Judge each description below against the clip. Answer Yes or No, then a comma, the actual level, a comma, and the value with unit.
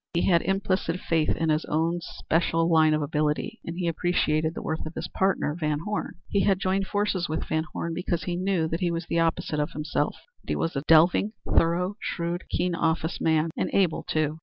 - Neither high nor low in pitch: Yes, medium, 165 Hz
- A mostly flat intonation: Yes, narrow, 2.3 semitones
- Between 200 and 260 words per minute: Yes, fast, 205 wpm